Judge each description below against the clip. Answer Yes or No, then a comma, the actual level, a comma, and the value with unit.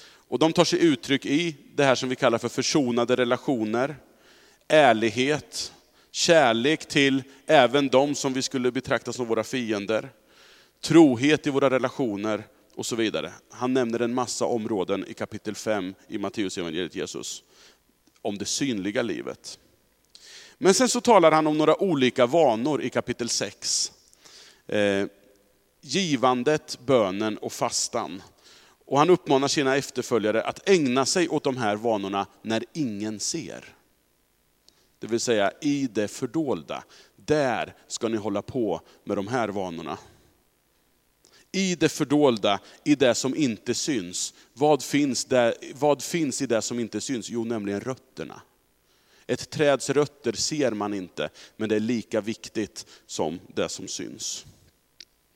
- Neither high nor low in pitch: No, low, 125 Hz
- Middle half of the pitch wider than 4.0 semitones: Yes, average, 5.0 semitones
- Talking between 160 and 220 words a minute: No, average, 140 wpm